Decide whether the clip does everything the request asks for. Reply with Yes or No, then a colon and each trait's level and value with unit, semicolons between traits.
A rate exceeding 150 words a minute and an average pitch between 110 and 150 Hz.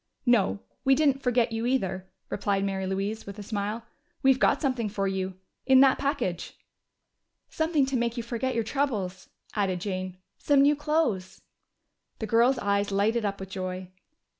No: average, 165 wpm; high, 220 Hz